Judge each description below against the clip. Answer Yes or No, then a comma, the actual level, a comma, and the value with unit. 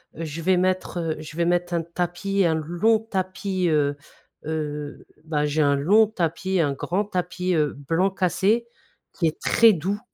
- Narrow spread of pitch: No, average, 3.2 semitones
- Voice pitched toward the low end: No, medium, 175 Hz